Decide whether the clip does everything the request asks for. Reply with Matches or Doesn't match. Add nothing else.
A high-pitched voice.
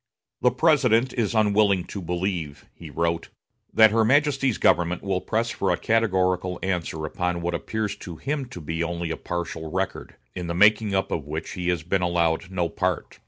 Doesn't match